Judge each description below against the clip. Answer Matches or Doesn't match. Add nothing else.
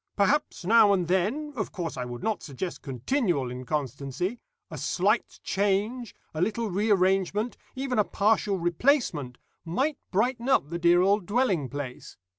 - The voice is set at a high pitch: Matches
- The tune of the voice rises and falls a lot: Matches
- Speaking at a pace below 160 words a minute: Matches